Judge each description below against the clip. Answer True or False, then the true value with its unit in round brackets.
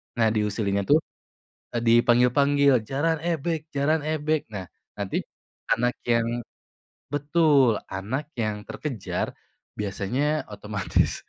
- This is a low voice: True (125 Hz)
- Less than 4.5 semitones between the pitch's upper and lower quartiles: False (5.6 semitones)